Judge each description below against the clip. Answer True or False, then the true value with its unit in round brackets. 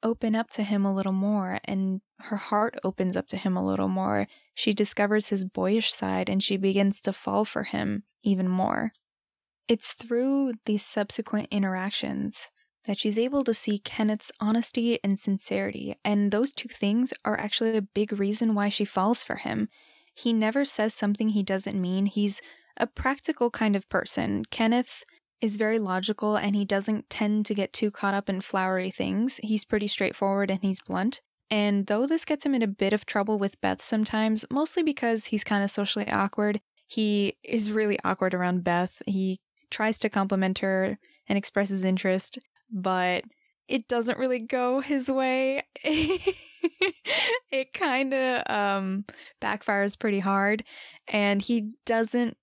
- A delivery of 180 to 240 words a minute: False (165 wpm)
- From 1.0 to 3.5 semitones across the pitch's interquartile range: True (3.0 semitones)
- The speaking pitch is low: False (210 Hz)